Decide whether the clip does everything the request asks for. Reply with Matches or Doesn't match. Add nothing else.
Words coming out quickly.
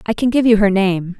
Matches